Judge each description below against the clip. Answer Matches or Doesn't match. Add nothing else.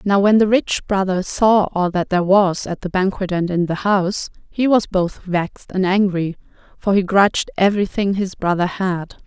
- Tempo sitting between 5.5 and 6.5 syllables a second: Doesn't match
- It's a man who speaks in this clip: Doesn't match